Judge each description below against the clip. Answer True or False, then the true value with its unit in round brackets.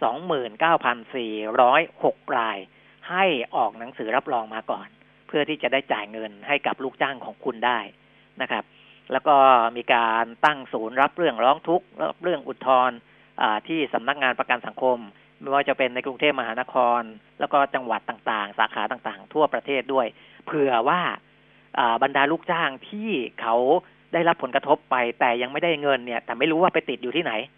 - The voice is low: True (130 Hz)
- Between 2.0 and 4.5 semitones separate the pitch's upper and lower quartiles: True (4.0 semitones)